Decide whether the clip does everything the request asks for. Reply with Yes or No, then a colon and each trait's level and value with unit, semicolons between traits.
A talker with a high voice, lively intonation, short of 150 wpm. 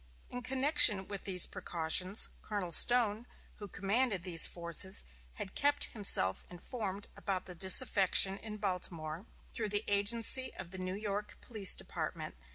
No: high, 200 Hz; average, 3.2 semitones; average, 140 wpm